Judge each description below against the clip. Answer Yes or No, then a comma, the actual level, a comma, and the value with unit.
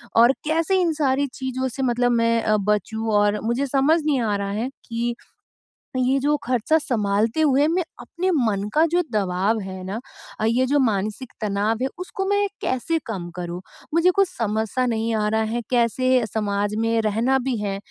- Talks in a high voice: Yes, high, 235 Hz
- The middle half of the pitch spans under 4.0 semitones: No, average, 4.3 semitones